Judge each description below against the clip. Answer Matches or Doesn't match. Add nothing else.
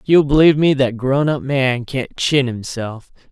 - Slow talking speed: Doesn't match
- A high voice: Doesn't match